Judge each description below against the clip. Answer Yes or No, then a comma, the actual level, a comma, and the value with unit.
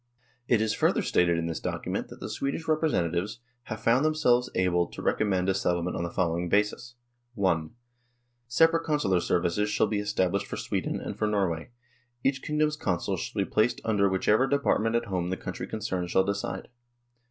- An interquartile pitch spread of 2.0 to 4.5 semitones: No, average, 5.3 semitones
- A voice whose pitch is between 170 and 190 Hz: No, low, 100 Hz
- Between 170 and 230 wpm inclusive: Yes, average, 190 wpm